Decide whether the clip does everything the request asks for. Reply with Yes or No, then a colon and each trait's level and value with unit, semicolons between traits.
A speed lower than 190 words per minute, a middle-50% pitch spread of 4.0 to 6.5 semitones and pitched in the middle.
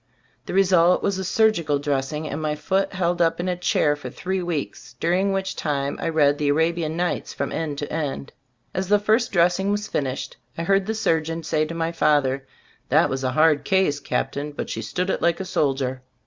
No: fast, 205 wpm; average, 4.3 semitones; medium, 165 Hz